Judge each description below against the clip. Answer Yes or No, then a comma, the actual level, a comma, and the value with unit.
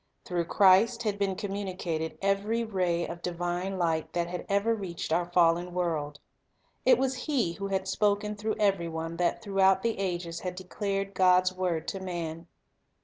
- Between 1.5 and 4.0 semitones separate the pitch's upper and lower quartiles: Yes, average, 2.7 semitones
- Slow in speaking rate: No, average, 165 wpm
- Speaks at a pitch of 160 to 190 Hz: Yes, medium, 185 Hz